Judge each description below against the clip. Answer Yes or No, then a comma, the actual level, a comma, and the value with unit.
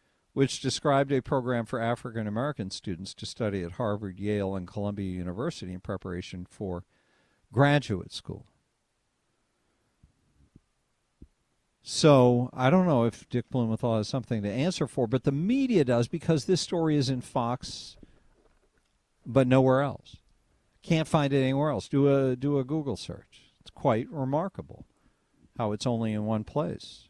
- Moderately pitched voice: No, low, 125 Hz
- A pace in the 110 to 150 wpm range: Yes, average, 145 wpm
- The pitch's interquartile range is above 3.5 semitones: Yes, average, 5.2 semitones